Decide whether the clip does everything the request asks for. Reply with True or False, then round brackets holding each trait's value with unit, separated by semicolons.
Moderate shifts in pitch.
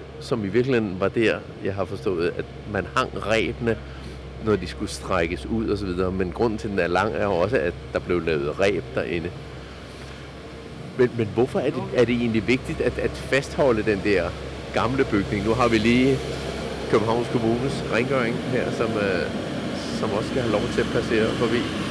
False (7.5 semitones)